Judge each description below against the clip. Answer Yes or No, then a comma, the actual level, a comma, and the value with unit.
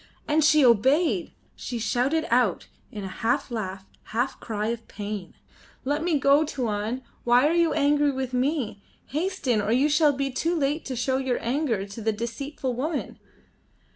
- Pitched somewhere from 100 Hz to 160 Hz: No, very high, 260 Hz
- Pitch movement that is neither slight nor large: Yes, average, 4.6 semitones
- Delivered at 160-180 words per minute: Yes, average, 170 wpm